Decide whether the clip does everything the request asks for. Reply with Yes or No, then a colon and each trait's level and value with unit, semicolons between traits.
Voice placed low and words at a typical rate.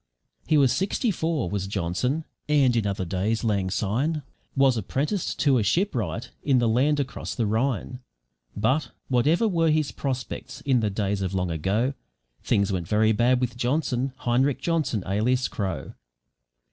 Yes: low, 120 Hz; average, 160 wpm